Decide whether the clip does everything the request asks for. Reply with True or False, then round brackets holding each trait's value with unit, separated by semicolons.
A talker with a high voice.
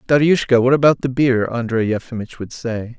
False (125 Hz)